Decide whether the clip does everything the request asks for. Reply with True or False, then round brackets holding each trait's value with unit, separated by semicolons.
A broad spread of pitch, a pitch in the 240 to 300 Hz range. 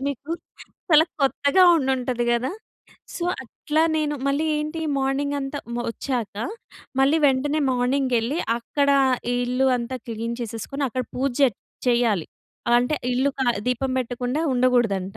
False (2.7 semitones; 260 Hz)